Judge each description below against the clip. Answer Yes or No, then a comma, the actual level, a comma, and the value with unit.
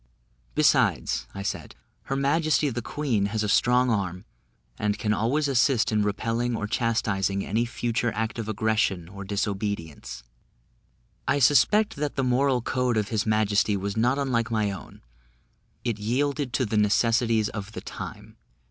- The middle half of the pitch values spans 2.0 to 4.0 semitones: Yes, average, 3.4 semitones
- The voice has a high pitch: No, low, 110 Hz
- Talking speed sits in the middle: Yes, average, 155 wpm